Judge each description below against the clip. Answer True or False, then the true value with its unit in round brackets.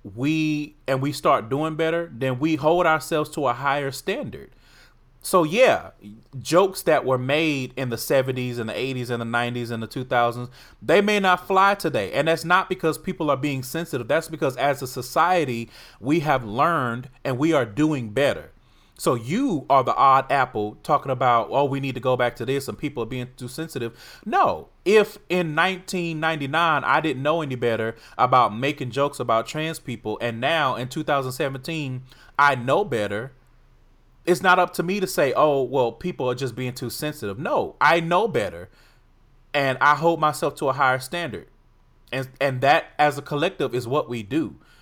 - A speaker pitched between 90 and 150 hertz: True (140 Hz)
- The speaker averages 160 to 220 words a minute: True (185 wpm)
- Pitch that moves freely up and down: False (4.2 semitones)